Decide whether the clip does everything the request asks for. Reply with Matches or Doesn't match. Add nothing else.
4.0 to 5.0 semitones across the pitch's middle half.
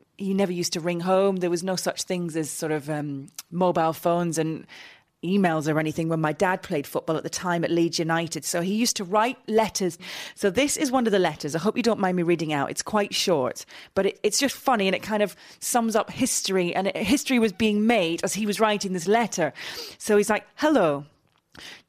Matches